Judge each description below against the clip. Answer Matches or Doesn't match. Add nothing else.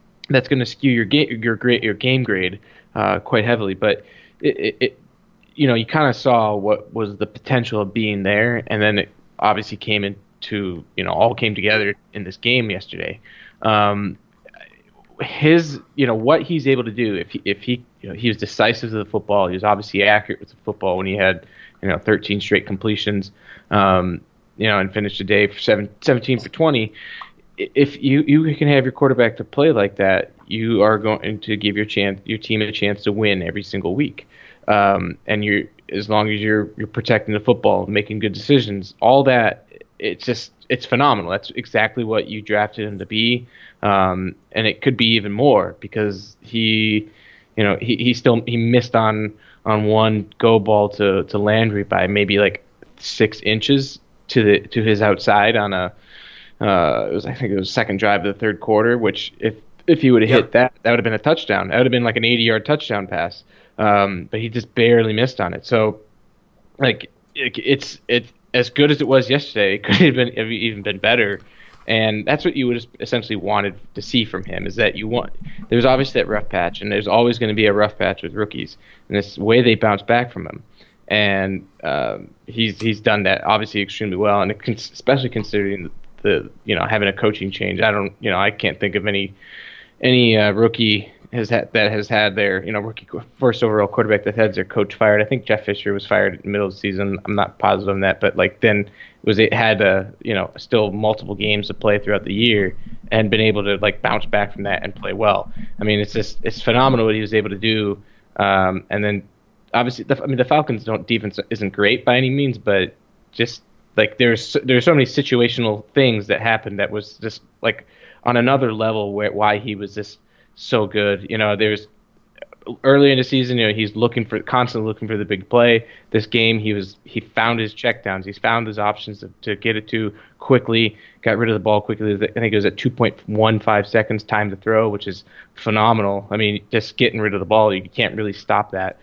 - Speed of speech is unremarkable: Doesn't match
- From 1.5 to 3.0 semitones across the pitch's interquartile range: Matches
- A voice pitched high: Doesn't match